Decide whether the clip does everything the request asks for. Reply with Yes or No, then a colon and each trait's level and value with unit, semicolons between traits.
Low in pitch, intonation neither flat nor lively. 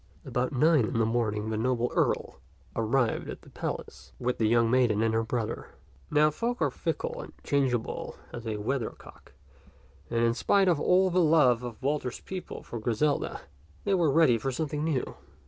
Yes: low, 125 Hz; average, 4.9 semitones